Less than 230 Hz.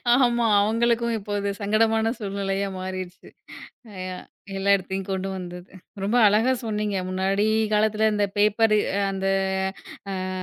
Yes: high, 205 Hz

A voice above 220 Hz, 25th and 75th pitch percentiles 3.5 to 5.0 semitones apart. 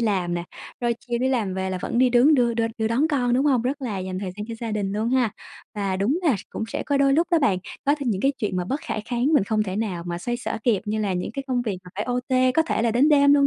Yes: high, 235 Hz; average, 4.7 semitones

